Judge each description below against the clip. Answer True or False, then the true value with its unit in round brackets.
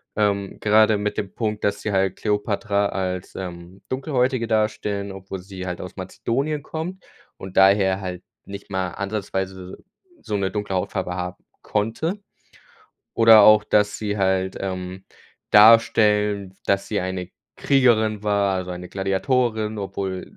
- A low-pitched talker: True (100 Hz)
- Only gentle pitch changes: True (2.3 semitones)